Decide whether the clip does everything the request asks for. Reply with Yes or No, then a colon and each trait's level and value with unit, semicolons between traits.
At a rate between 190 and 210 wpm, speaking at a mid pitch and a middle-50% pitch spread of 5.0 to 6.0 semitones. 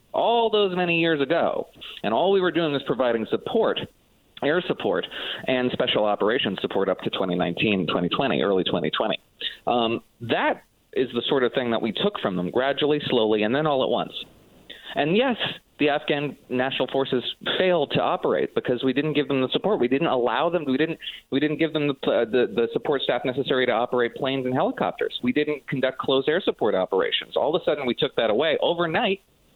Yes: average, 200 wpm; medium, 150 Hz; wide, 5.5 semitones